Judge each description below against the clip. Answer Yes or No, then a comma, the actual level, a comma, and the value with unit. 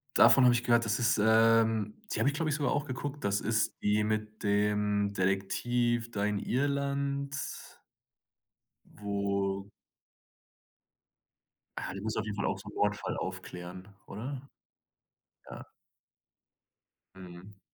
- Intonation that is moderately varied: Yes, average, 3.4 semitones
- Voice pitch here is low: Yes, low, 110 Hz